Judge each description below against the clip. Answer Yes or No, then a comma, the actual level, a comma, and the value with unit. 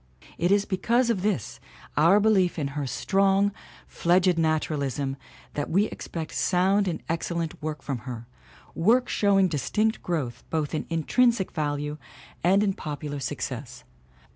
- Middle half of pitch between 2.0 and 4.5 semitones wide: No, average, 5.1 semitones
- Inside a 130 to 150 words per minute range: Yes, average, 140 wpm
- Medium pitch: Yes, medium, 165 Hz